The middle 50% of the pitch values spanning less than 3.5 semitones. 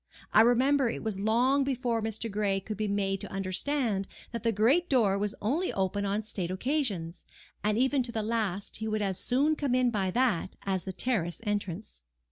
No: average, 4.2 semitones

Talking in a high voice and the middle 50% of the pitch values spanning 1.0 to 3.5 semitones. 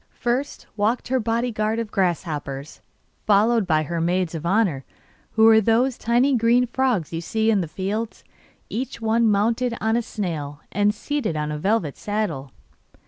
No: high, 215 Hz; average, 5.2 semitones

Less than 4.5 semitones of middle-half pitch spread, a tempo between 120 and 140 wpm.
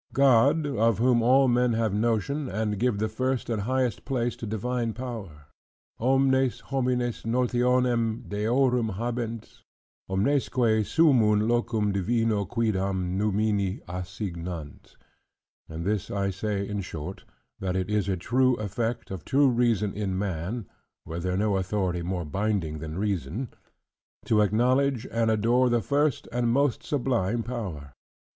Yes: average, 4.0 semitones; slow, 135 wpm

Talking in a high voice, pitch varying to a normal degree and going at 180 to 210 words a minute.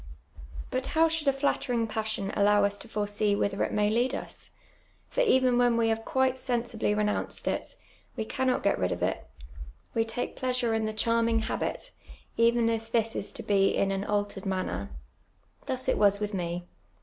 Yes: high, 225 Hz; average, 3.1 semitones; average, 185 wpm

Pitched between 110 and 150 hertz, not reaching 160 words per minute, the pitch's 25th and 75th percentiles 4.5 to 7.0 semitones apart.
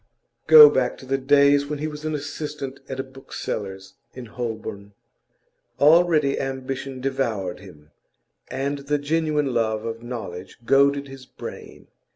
No: low, 135 Hz; average, 140 wpm; average, 3.7 semitones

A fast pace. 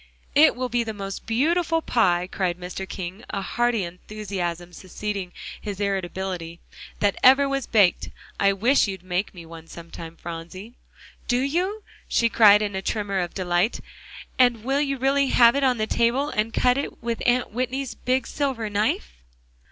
No: average, 165 wpm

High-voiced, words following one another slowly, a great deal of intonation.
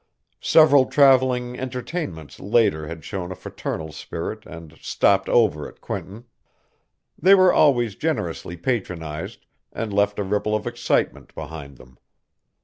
No: low, 105 Hz; slow, 130 wpm; wide, 7.2 semitones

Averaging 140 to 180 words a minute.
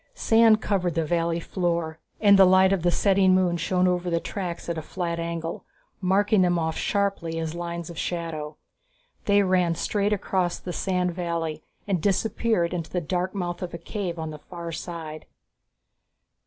Yes: average, 175 wpm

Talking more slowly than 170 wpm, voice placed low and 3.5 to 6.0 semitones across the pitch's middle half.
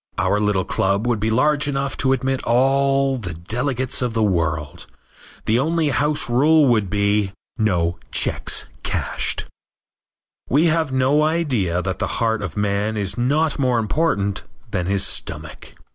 Yes: average, 150 wpm; low, 120 Hz; wide, 5.4 semitones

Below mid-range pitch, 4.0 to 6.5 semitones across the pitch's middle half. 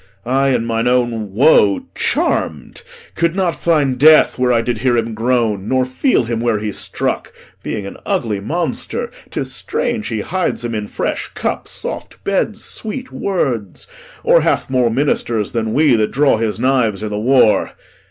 Yes: low, 120 Hz; average, 4.5 semitones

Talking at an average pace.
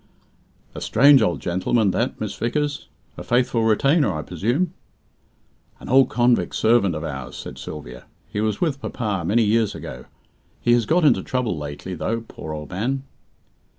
Yes: average, 160 wpm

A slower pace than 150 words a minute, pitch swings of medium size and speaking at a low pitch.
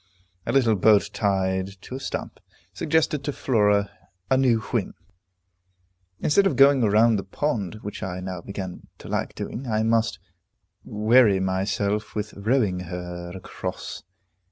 Yes: average, 140 wpm; average, 4.3 semitones; low, 105 Hz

